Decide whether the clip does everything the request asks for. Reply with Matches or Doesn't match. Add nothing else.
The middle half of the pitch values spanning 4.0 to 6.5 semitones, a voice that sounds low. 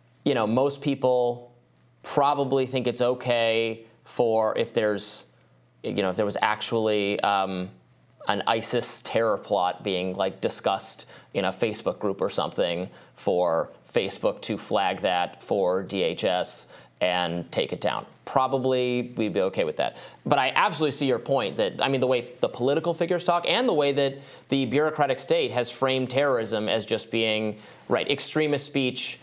Matches